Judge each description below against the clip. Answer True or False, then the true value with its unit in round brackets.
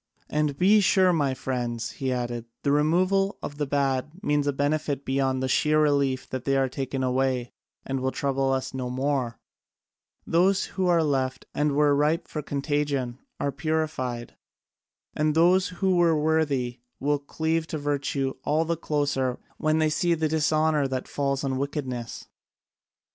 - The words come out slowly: False (160 wpm)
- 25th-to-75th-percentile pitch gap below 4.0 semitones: True (2.9 semitones)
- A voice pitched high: False (145 Hz)